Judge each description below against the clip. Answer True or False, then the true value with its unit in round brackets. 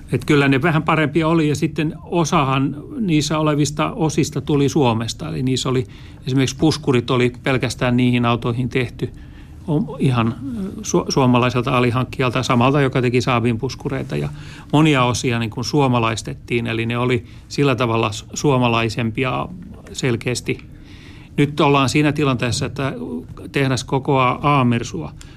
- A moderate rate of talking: True (130 wpm)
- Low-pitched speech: True (130 Hz)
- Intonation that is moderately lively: True (3.1 semitones)